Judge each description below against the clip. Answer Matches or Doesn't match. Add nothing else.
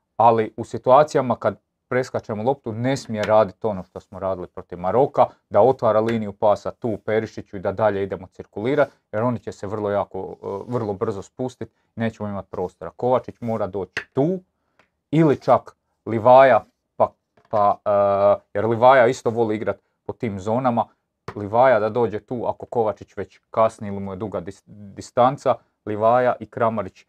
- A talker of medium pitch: Doesn't match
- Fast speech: Matches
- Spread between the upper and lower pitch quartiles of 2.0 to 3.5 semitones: Matches